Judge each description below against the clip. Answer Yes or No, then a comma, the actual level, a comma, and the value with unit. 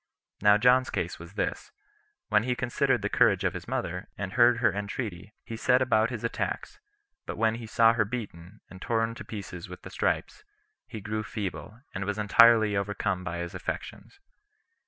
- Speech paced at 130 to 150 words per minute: No, average, 180 wpm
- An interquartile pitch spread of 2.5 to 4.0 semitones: Yes, average, 2.8 semitones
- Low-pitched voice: Yes, low, 110 Hz